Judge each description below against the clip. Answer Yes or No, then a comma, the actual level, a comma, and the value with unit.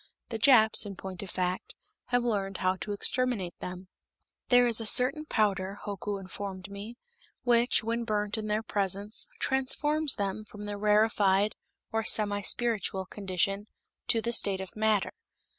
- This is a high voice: Yes, high, 210 Hz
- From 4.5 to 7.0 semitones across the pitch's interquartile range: No, average, 3.0 semitones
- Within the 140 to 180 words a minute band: Yes, average, 155 wpm